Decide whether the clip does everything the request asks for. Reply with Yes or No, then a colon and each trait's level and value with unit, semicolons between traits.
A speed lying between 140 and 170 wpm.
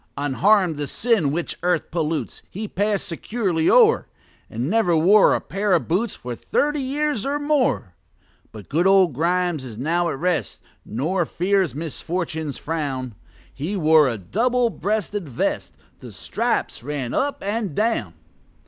Yes: average, 150 wpm